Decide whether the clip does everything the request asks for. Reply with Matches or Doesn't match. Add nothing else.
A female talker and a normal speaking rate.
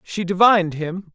Doesn't match